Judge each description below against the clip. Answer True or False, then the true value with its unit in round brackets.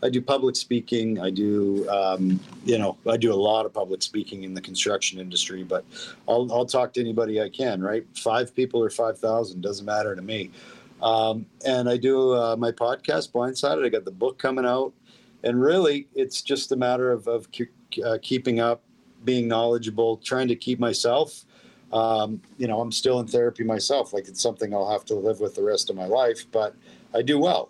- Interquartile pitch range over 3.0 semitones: False (2.7 semitones)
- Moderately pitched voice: False (120 Hz)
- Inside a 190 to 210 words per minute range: True (200 wpm)